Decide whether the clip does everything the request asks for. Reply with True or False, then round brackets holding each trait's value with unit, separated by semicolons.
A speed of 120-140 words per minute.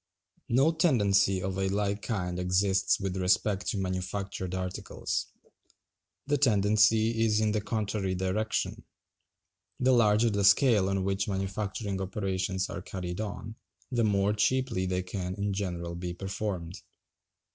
True (135 wpm)